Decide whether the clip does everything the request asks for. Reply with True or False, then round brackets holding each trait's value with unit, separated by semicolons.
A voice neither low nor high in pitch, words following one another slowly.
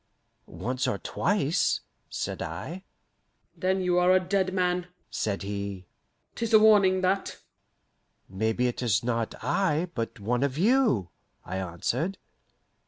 True (160 Hz; 130 wpm)